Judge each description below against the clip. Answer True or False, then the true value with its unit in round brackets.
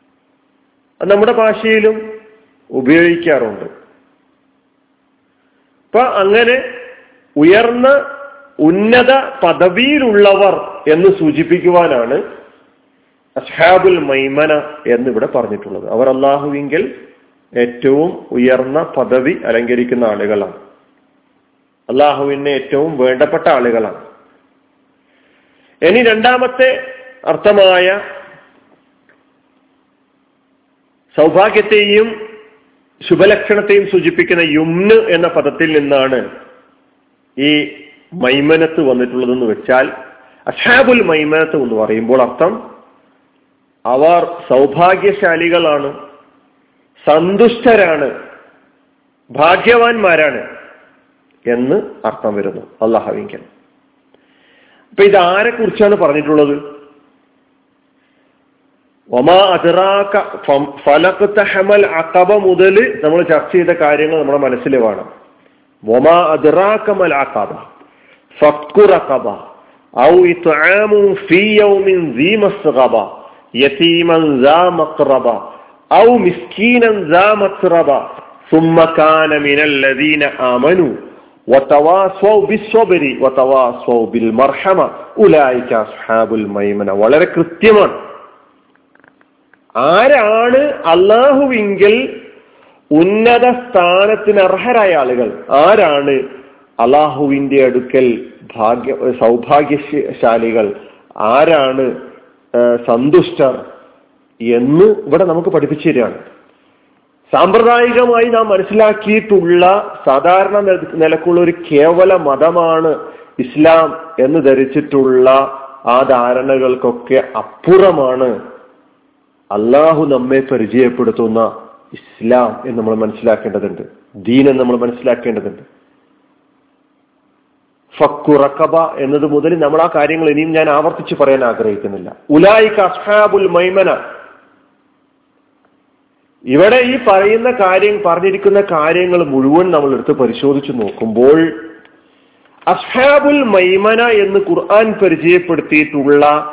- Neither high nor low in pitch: True (180 Hz)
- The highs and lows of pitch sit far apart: True (8.5 semitones)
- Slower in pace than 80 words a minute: True (70 wpm)